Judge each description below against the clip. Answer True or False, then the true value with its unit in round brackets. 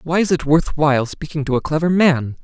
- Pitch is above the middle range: False (150 Hz)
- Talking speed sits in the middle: False (245 wpm)